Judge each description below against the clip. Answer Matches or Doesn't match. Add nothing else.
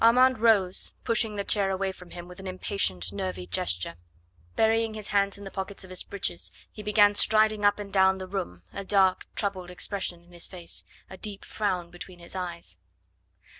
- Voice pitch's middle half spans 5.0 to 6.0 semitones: Doesn't match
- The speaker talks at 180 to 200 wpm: Matches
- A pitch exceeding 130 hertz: Matches